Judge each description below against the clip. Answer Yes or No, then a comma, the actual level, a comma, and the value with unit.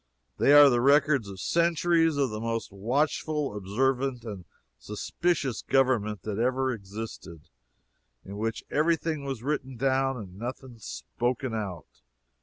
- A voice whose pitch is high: No, low, 125 Hz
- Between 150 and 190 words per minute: No, slow, 135 wpm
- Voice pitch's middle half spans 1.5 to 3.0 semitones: No, average, 4.7 semitones